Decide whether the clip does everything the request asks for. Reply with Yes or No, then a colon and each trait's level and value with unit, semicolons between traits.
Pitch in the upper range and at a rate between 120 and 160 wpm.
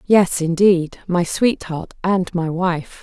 No: medium, 180 Hz; average, 140 wpm